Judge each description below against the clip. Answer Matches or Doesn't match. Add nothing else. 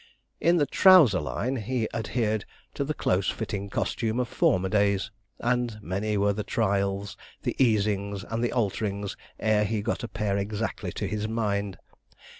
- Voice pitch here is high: Doesn't match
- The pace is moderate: Matches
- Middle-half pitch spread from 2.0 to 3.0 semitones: Matches